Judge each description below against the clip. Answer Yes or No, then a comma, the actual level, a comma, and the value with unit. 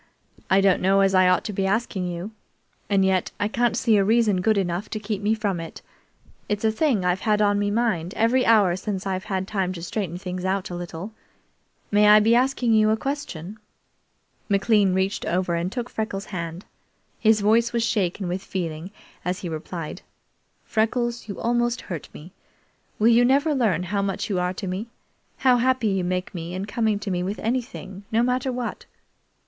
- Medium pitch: No, high, 200 Hz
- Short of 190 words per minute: No, average, 195 wpm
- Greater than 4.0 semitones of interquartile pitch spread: No, average, 3.5 semitones